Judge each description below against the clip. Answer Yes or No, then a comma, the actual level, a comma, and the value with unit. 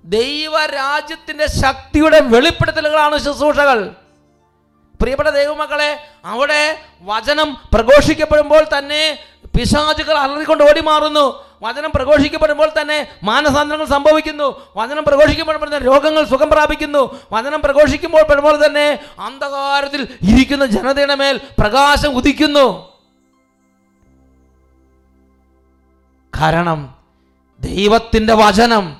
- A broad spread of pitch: Yes, wide, 6.3 semitones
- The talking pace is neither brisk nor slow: No, slow, 80 wpm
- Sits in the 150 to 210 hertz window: No, very high, 285 Hz